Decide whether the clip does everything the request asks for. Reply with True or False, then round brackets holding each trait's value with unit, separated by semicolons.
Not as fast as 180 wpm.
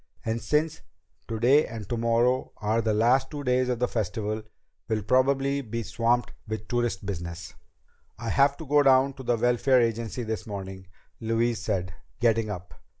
True (160 wpm)